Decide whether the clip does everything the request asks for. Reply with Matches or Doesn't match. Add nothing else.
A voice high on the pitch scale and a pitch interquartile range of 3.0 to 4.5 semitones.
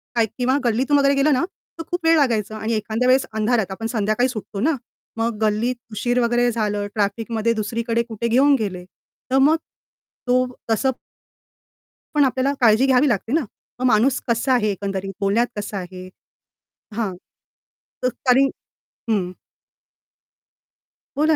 Matches